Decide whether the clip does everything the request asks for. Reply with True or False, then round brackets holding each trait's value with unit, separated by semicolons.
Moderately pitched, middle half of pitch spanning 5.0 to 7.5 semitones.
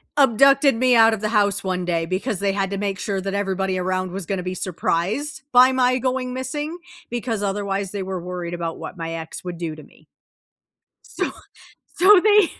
False (200 Hz; 5.6 semitones)